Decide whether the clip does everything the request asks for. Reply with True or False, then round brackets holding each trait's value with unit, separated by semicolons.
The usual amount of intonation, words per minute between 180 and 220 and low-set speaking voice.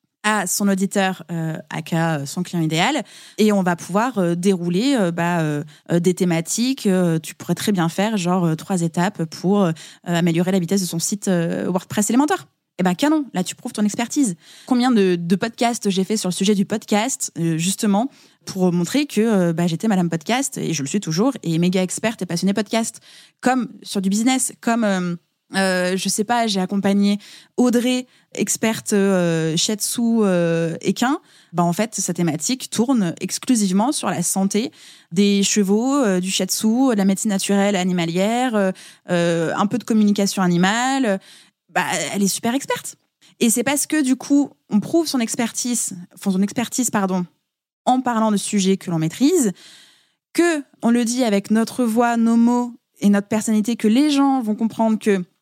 False (4.5 semitones; 185 wpm; 200 Hz)